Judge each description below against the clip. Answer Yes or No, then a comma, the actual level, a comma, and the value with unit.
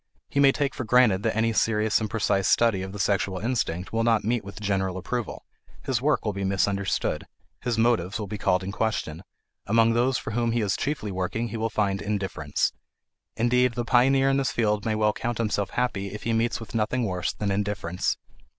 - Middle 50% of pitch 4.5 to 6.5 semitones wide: No, average, 3.2 semitones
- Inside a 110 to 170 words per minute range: No, fast, 205 wpm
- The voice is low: Yes, low, 110 Hz